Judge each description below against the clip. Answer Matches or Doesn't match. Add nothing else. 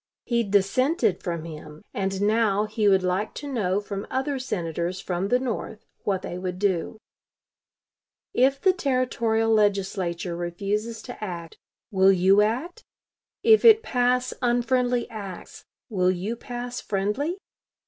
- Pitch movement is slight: Doesn't match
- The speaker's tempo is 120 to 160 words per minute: Matches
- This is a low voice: Doesn't match